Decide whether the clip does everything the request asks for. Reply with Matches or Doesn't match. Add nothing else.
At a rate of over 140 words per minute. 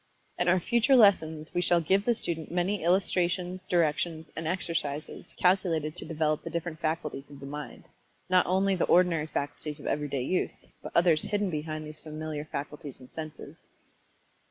Matches